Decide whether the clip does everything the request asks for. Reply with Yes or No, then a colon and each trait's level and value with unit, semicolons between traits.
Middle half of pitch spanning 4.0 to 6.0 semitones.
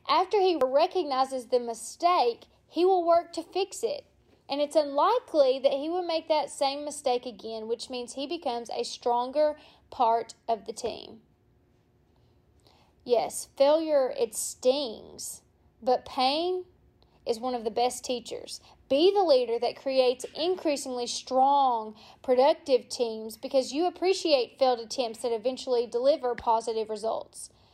Yes: average, 5.1 semitones